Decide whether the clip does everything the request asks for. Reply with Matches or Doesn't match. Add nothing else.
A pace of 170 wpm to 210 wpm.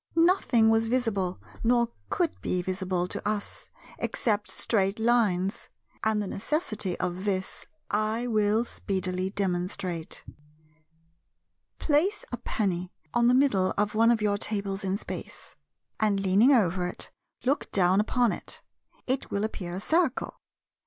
Doesn't match